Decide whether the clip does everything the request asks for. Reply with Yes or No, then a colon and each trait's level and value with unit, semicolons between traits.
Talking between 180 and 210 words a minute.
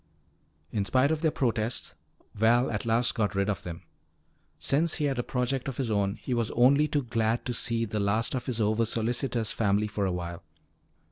Yes: average, 190 wpm